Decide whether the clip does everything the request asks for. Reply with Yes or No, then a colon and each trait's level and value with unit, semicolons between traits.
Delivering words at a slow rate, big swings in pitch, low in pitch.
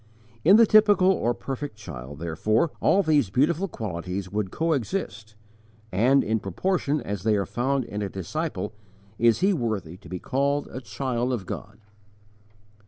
No: average, 155 wpm; wide, 6.8 semitones; low, 115 Hz